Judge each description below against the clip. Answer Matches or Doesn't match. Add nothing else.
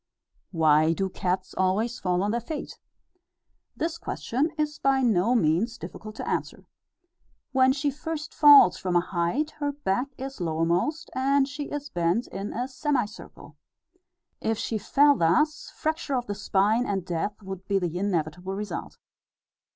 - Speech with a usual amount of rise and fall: Doesn't match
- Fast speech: Doesn't match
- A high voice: Matches